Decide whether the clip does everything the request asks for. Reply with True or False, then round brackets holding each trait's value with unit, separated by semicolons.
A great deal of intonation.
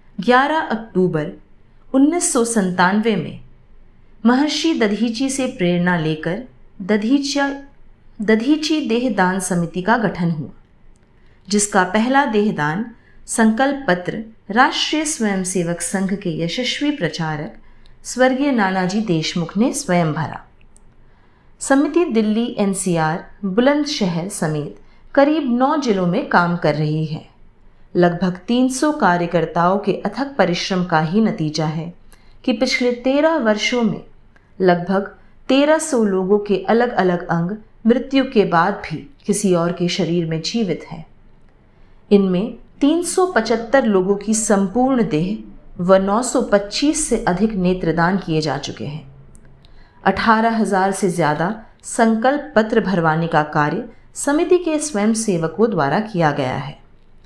True (6.0 semitones)